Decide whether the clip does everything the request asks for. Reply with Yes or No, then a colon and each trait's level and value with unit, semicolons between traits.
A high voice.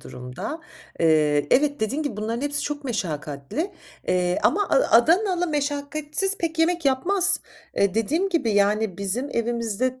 Yes: very high, 265 Hz